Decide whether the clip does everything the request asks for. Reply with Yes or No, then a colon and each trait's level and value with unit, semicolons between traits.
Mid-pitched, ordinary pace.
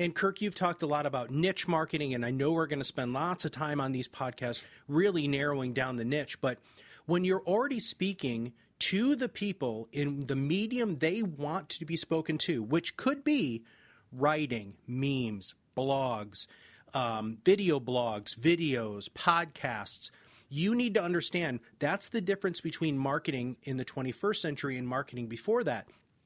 Yes: medium, 145 Hz; average, 160 wpm